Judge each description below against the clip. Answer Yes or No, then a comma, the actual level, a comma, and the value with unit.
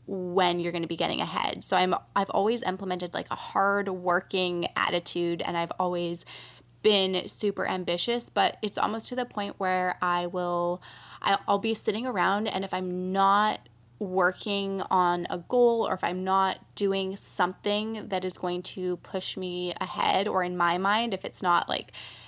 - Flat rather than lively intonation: Yes, narrow, 2.1 semitones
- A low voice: No, medium, 185 Hz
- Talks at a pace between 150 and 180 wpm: Yes, average, 175 wpm